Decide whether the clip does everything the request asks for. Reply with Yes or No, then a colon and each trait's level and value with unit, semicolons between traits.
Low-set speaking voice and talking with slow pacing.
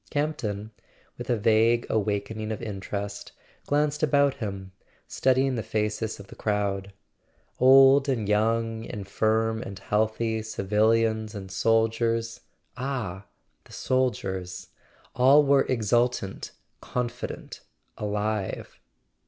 Yes: low, 110 Hz; slow, 100 wpm